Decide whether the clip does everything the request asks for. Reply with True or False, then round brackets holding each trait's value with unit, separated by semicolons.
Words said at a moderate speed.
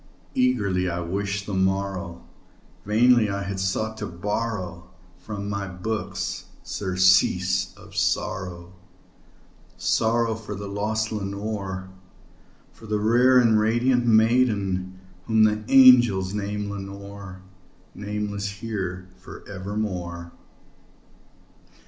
False (100 wpm)